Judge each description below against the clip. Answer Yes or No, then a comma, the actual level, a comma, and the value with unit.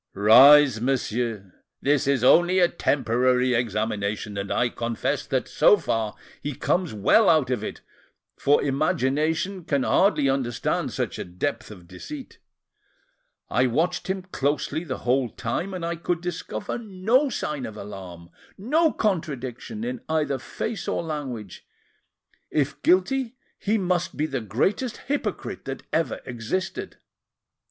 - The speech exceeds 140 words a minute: No, slow, 135 wpm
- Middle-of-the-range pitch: Yes, medium, 145 Hz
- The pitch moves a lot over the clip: Yes, wide, 7.4 semitones